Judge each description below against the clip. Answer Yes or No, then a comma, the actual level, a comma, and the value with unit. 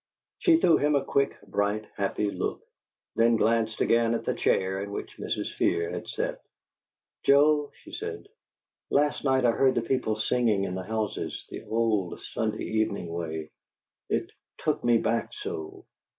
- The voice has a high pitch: No, low, 115 Hz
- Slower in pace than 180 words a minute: Yes, average, 160 wpm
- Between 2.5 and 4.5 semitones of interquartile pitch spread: No, wide, 5.4 semitones